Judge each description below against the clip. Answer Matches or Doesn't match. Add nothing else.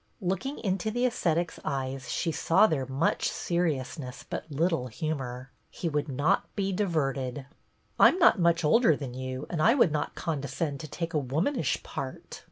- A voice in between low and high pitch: Matches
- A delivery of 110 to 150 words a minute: Doesn't match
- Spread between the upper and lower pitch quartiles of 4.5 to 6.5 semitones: Matches